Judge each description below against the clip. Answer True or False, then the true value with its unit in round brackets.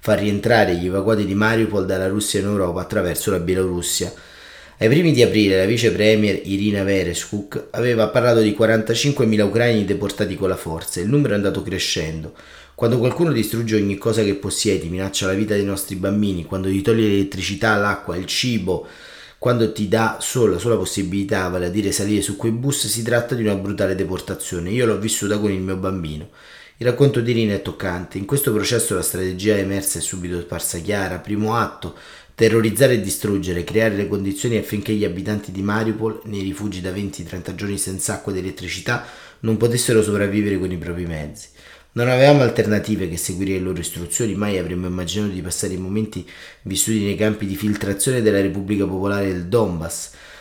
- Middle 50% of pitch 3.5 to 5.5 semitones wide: False (2.8 semitones)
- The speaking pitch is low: True (100 Hz)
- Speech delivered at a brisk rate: True (185 wpm)